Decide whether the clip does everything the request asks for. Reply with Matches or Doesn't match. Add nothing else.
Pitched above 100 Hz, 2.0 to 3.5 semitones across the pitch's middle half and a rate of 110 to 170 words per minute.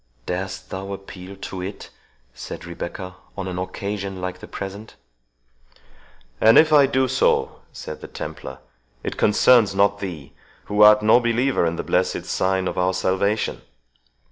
Doesn't match